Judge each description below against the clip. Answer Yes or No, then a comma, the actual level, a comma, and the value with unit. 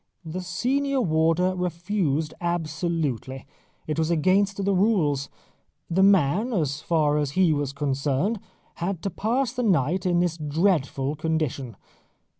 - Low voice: No, medium, 165 Hz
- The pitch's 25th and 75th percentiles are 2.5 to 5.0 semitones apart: Yes, average, 4.4 semitones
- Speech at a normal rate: No, slow, 130 wpm